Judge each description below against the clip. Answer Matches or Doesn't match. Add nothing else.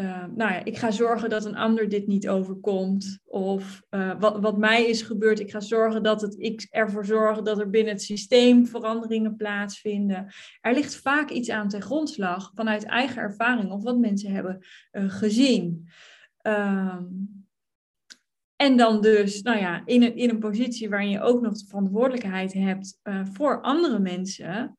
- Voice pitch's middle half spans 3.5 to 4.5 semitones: Doesn't match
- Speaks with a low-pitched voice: Doesn't match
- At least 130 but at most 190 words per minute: Matches